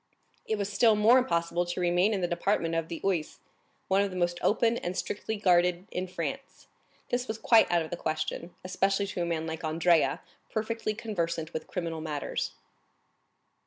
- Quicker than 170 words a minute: Yes, average, 180 wpm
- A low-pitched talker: No, medium, 180 Hz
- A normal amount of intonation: Yes, average, 3.8 semitones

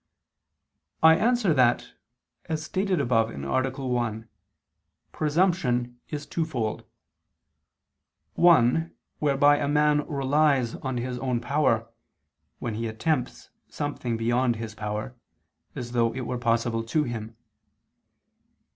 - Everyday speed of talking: No, slow, 110 wpm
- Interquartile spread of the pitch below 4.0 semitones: No, average, 4.3 semitones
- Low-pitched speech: Yes, low, 125 Hz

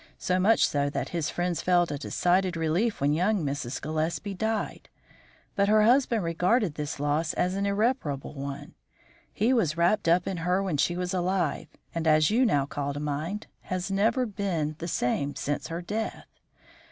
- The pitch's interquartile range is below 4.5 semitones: No, average, 4.8 semitones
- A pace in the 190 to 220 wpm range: No, average, 180 wpm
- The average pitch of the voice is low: No, medium, 175 Hz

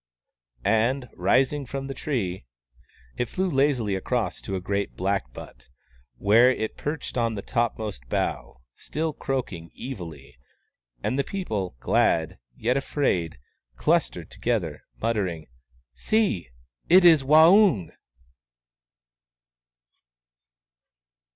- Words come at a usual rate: No, slow, 110 wpm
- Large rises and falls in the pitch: Yes, wide, 7.4 semitones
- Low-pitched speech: Yes, low, 110 Hz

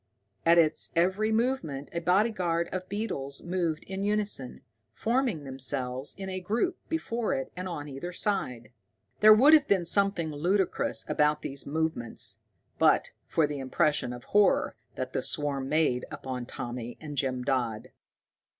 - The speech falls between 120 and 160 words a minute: Yes, average, 150 wpm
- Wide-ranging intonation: Yes, wide, 6.5 semitones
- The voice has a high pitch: No, medium, 165 Hz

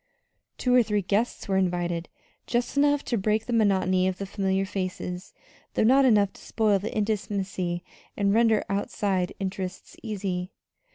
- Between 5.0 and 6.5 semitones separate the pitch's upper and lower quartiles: No, average, 2.8 semitones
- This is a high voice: Yes, high, 200 Hz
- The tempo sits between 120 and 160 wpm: Yes, average, 155 wpm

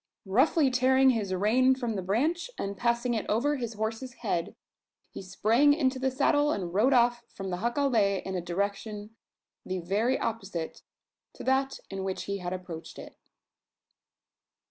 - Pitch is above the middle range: Yes, high, 225 Hz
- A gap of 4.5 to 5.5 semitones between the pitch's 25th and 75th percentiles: Yes, average, 5.1 semitones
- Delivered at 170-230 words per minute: No, average, 160 wpm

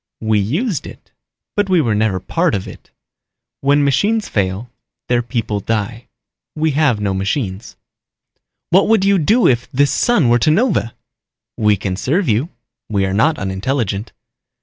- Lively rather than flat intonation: Yes, wide, 7.4 semitones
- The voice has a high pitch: No, low, 120 Hz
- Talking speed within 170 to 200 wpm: No, average, 155 wpm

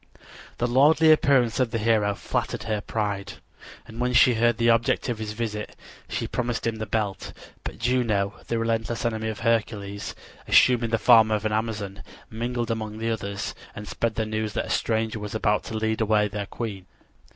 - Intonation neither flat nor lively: No, narrow, 1.8 semitones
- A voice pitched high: No, low, 110 Hz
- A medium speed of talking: Yes, average, 185 wpm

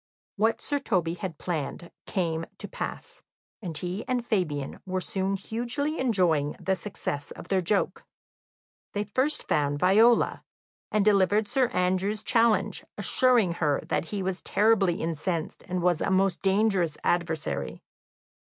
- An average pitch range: Yes, average, 4.1 semitones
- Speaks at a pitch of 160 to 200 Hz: Yes, high, 190 Hz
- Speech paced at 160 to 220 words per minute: No, average, 140 wpm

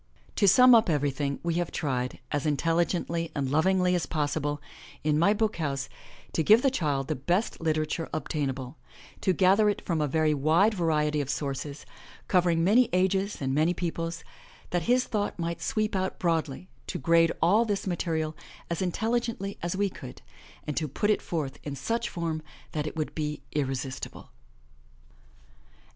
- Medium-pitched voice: Yes, medium, 165 Hz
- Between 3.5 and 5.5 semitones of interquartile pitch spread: Yes, average, 4.2 semitones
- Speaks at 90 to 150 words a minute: No, average, 165 wpm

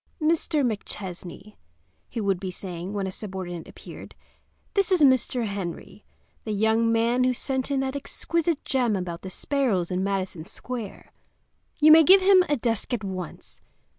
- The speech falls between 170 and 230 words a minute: No, average, 160 wpm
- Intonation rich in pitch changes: Yes, wide, 6.2 semitones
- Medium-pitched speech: No, high, 225 Hz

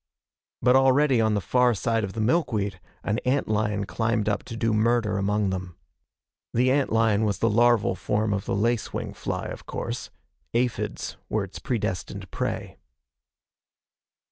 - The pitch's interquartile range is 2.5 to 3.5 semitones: Yes, average, 2.8 semitones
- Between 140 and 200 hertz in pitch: No, low, 110 Hz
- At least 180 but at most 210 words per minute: No, average, 155 wpm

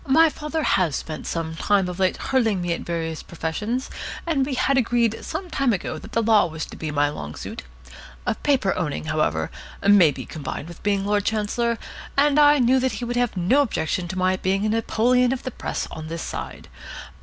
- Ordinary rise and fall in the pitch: No, wide, 6.9 semitones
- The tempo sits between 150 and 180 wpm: No, average, 200 wpm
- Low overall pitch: No, high, 205 Hz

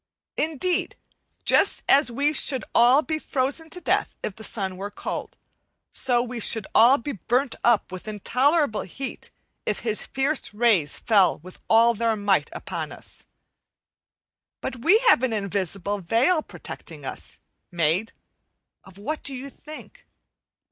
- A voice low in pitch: No, high, 235 Hz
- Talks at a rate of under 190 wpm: Yes, average, 145 wpm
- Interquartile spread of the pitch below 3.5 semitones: No, wide, 5.4 semitones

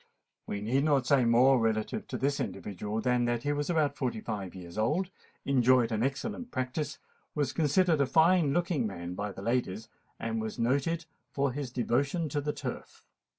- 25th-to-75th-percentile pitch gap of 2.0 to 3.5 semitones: No, average, 4.5 semitones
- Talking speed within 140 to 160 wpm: No, average, 185 wpm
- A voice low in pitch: Yes, low, 130 Hz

